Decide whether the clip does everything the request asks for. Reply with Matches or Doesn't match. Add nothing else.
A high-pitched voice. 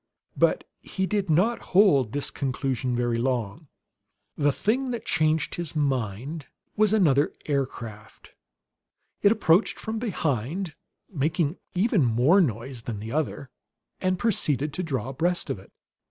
Doesn't match